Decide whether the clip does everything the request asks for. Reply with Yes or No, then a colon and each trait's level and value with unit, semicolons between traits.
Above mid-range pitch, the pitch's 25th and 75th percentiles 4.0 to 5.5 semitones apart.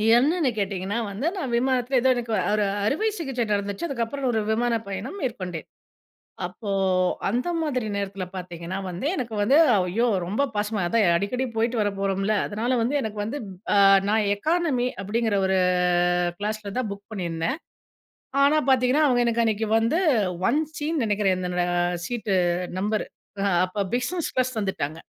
Yes: high, 220 Hz; average, 4.3 semitones